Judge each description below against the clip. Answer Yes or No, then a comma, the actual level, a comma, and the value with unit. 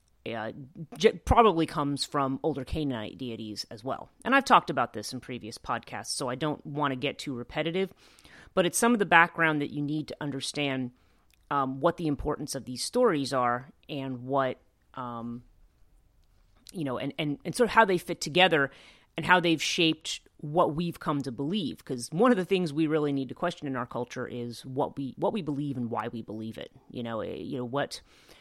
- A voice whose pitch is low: No, medium, 145 Hz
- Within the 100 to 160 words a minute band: No, fast, 205 wpm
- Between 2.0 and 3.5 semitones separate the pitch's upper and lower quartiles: No, average, 4.8 semitones